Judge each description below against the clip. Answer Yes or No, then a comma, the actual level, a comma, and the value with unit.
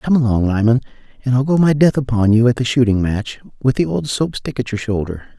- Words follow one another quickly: Yes, fast, 245 wpm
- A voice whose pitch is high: No, low, 120 Hz